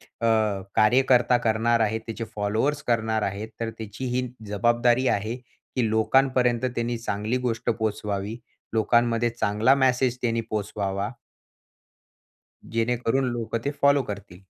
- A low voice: Yes, low, 115 Hz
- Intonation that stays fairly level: Yes, narrow, 2.3 semitones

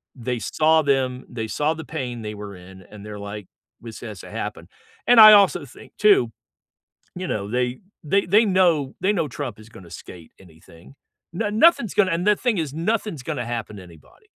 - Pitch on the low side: Yes, low, 130 Hz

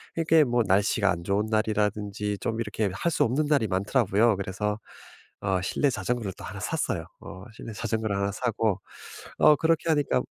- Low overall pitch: Yes, low, 110 Hz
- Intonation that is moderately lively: Yes, average, 3.5 semitones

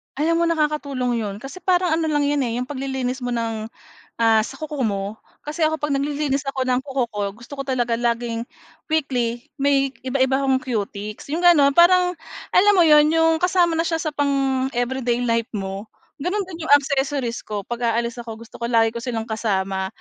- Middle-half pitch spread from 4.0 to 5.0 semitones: Yes, average, 4.3 semitones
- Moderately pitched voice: No, very high, 265 Hz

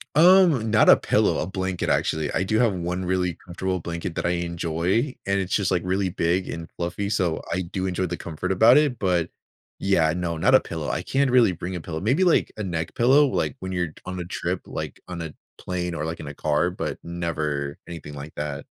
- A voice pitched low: Yes, very low, 90 Hz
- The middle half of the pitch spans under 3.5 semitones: Yes, average, 2.7 semitones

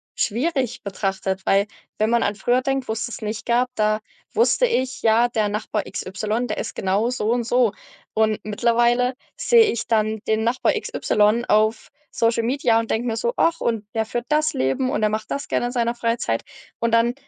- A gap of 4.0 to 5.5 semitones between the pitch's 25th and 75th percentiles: No, narrow, 2.4 semitones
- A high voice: Yes, high, 230 Hz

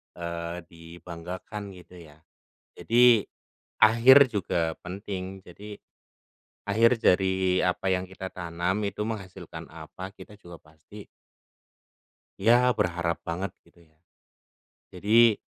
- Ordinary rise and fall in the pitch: Yes, average, 3.6 semitones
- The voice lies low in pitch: Yes, very low, 95 Hz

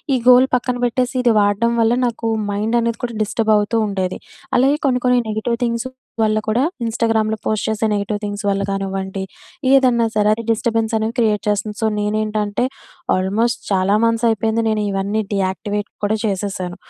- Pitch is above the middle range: Yes, high, 215 Hz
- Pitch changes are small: Yes, narrow, 2.3 semitones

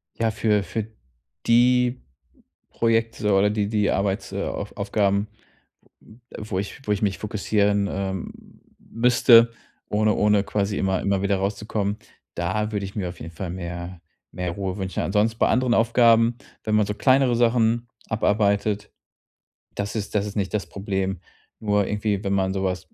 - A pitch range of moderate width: No, narrow, 2.3 semitones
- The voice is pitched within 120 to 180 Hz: No, low, 105 Hz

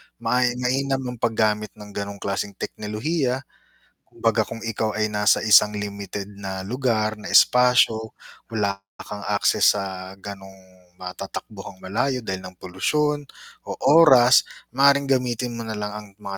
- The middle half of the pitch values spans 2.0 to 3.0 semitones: No, average, 3.8 semitones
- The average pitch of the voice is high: No, low, 110 Hz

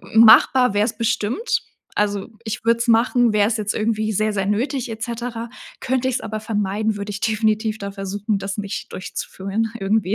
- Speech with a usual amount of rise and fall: No, narrow, 2.0 semitones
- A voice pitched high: Yes, high, 215 Hz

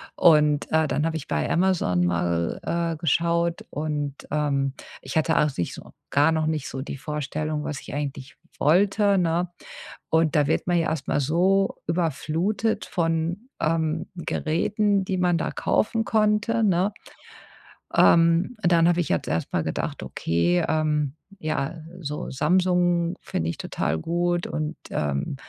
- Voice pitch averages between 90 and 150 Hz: No, medium, 160 Hz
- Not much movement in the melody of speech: No, average, 3.2 semitones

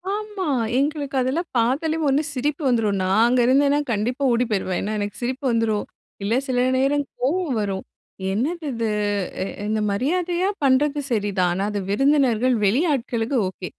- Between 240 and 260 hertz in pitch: Yes, very high, 255 Hz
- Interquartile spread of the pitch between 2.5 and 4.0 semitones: No, average, 5.1 semitones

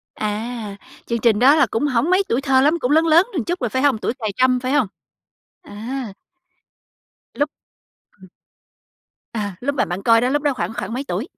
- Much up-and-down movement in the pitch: No, average, 4.2 semitones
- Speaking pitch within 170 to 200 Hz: No, very high, 255 Hz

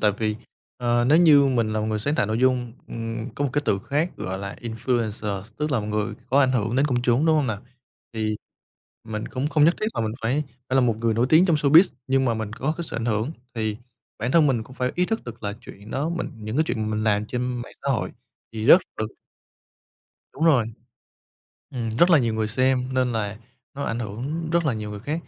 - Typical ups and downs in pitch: Yes, average, 4.4 semitones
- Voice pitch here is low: Yes, low, 120 Hz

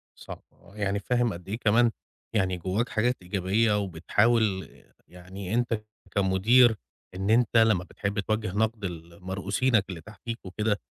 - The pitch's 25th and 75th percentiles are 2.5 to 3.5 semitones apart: Yes, average, 3.2 semitones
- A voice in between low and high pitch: No, low, 105 Hz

